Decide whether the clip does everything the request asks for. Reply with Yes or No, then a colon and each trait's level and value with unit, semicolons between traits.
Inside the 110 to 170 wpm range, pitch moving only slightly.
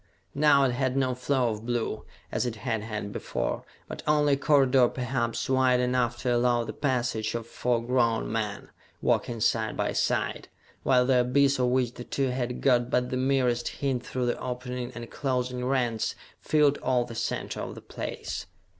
No: average, 180 wpm; narrow, 1.7 semitones